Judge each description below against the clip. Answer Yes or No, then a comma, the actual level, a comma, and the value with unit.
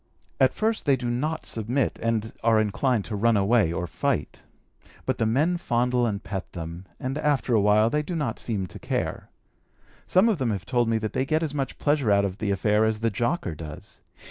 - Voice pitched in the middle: No, low, 115 Hz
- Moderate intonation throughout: Yes, average, 4.6 semitones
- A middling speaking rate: No, fast, 210 wpm